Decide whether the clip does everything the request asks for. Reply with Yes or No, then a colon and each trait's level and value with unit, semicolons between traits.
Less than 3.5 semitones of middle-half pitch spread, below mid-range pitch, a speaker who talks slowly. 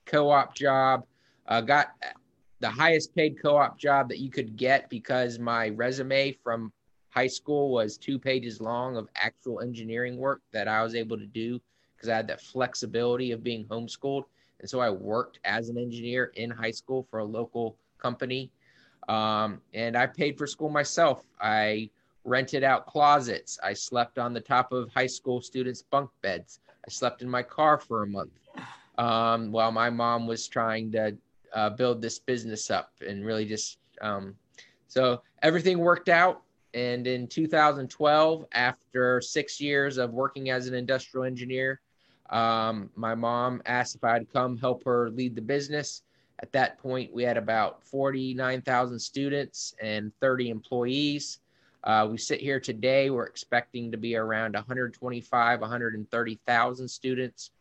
No: average, 2.7 semitones; low, 125 Hz; average, 165 wpm